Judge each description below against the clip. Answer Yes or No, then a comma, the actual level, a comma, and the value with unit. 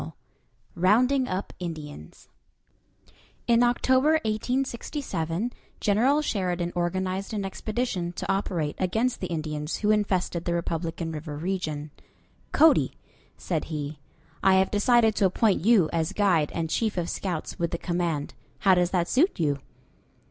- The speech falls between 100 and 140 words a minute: Yes, slow, 135 wpm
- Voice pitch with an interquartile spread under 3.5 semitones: No, average, 4.7 semitones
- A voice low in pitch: No, medium, 185 Hz